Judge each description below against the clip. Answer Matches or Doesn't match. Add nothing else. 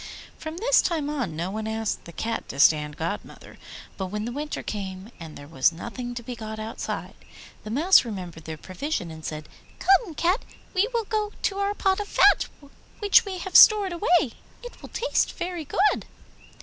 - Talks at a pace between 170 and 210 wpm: Matches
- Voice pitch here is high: Matches